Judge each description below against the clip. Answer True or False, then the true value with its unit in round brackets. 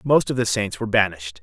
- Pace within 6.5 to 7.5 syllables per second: True (6.8 syllables/s)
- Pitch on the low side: True (105 Hz)